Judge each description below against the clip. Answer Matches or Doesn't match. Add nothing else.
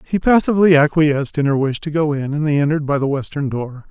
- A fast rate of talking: Matches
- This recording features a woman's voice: Doesn't match